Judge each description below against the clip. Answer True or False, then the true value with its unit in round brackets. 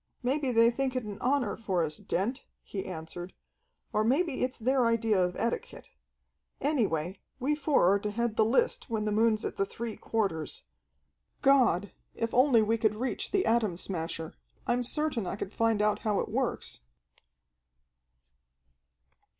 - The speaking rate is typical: True (160 wpm)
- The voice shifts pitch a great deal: False (4.2 semitones)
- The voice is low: False (225 Hz)